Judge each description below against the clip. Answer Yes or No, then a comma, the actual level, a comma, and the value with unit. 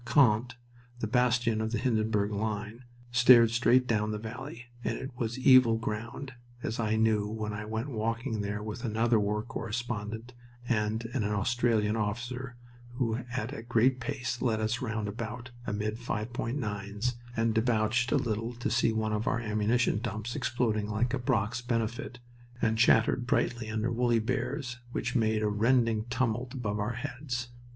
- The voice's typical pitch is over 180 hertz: No, low, 115 Hz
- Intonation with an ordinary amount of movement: No, narrow, 2.2 semitones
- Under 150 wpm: No, average, 160 wpm